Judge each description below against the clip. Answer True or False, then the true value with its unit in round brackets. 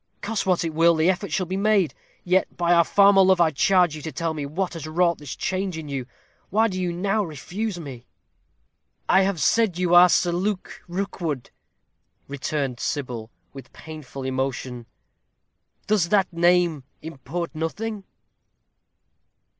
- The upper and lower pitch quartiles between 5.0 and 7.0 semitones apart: False (4.0 semitones)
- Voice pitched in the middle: True (170 Hz)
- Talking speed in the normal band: True (155 wpm)